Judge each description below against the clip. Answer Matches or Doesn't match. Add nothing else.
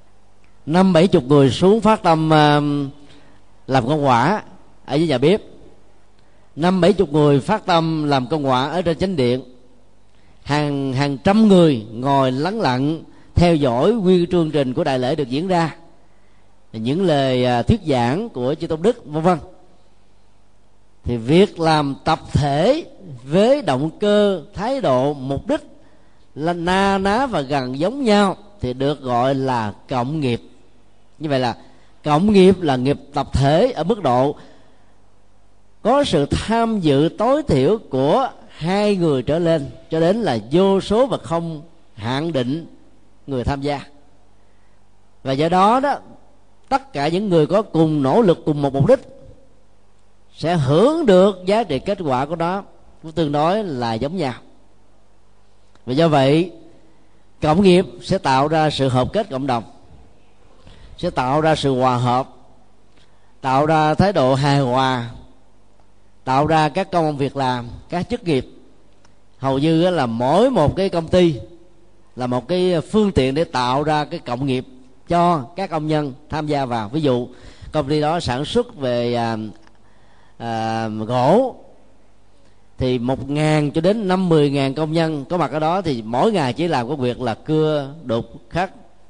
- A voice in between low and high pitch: Matches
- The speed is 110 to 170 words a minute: Matches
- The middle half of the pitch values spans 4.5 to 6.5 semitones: Matches